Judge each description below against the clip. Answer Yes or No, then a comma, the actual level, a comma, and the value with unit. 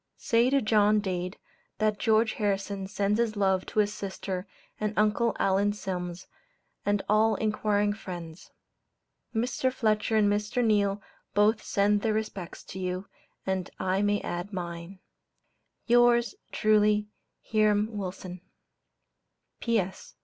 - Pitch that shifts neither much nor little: No, narrow, 2.1 semitones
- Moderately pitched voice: No, high, 205 Hz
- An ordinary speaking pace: No, slow, 125 wpm